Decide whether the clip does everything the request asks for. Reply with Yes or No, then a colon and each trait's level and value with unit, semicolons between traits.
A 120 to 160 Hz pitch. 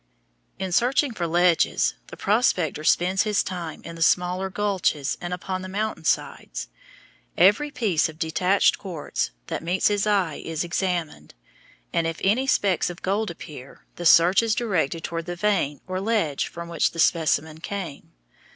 No: medium, 180 Hz